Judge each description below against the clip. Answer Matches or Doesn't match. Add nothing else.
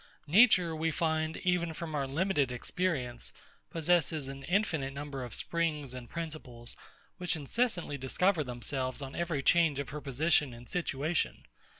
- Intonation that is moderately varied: Matches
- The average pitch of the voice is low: Doesn't match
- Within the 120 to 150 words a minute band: Matches